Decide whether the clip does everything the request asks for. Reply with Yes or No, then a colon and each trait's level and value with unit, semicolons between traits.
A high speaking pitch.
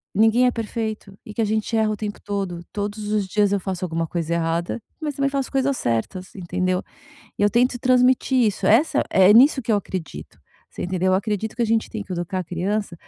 Yes: high, 205 Hz